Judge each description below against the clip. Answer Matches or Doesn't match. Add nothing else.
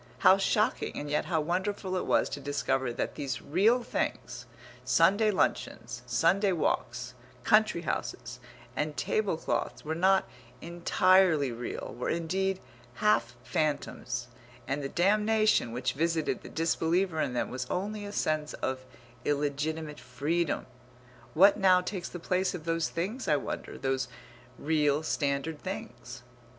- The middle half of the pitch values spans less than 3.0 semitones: Doesn't match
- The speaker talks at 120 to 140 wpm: Matches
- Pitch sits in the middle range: Matches